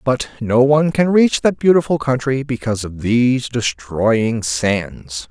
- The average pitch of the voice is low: Yes, low, 125 Hz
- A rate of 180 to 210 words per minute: No, average, 145 wpm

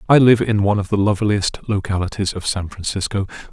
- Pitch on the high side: No, low, 100 Hz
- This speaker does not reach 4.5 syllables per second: No, 6.3 syllables/s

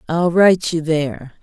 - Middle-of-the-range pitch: Yes, medium, 165 Hz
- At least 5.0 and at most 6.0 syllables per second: Yes, 5.1 syllables/s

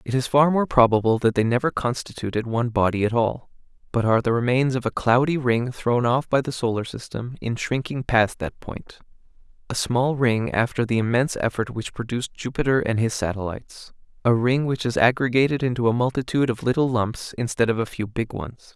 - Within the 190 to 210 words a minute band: Yes, average, 200 wpm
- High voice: No, low, 120 Hz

